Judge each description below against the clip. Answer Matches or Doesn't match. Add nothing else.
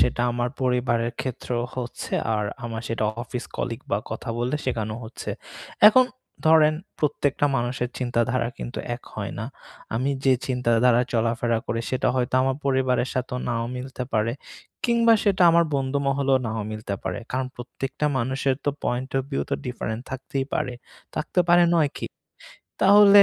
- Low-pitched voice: Matches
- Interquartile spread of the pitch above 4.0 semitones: Doesn't match